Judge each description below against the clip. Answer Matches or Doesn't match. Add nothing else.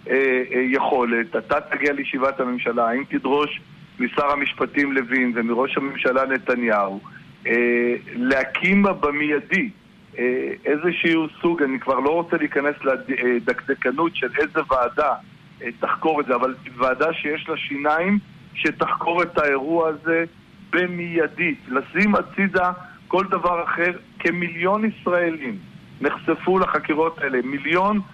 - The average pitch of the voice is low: Doesn't match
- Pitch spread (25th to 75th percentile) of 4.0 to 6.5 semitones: Matches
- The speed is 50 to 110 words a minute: Matches